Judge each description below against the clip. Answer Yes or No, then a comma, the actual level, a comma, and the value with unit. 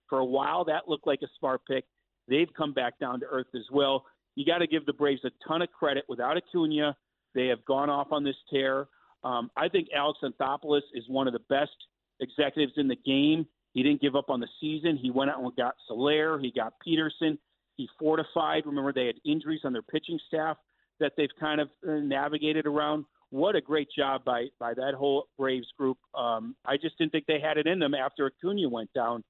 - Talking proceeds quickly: Yes, fast, 220 wpm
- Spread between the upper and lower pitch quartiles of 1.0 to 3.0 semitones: Yes, narrow, 2.6 semitones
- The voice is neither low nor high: Yes, medium, 145 Hz